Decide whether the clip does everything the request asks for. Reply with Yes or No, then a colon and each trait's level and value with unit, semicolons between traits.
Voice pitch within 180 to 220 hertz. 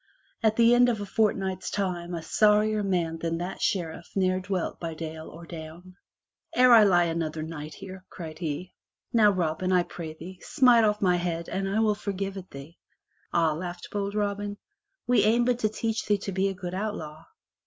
Yes: medium, 185 Hz